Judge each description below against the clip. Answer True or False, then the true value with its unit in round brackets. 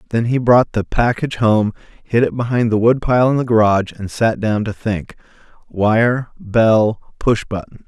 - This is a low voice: True (115 Hz)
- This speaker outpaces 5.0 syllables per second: False (4.9 syllables/s)